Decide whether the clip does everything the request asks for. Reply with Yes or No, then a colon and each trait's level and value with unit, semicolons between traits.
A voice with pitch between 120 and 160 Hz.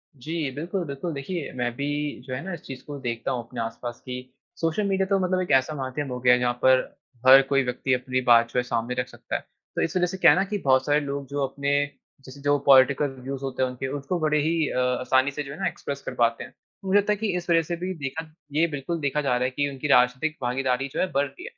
Yes: medium, 140 Hz